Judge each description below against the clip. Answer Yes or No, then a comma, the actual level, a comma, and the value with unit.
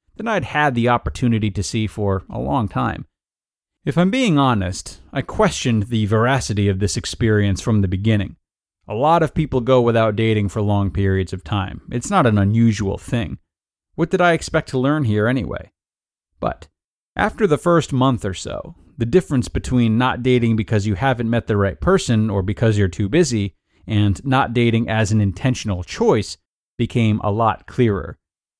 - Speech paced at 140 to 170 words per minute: No, average, 180 wpm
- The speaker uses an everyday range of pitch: Yes, average, 4.2 semitones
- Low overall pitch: Yes, low, 110 Hz